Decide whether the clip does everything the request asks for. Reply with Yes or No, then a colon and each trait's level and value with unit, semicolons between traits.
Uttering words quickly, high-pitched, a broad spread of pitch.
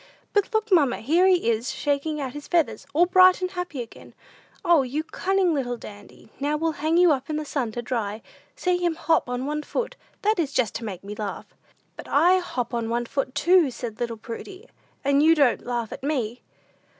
Yes: fast, 210 wpm; very high, 285 Hz; wide, 6.2 semitones